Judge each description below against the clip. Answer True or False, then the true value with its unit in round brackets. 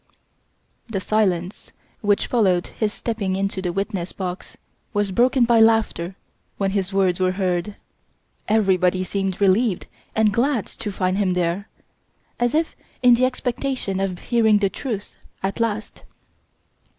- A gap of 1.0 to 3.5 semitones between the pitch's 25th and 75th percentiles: True (3.2 semitones)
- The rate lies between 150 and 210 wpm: False (140 wpm)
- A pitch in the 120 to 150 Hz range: False (200 Hz)